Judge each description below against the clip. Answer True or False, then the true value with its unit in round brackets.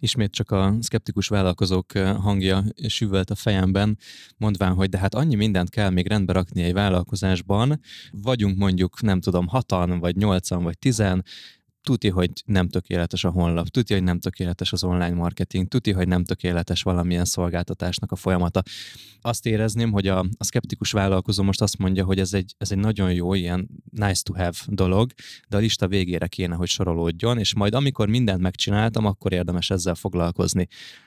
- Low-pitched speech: True (95 Hz)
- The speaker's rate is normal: False (170 wpm)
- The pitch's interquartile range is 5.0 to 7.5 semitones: False (2.7 semitones)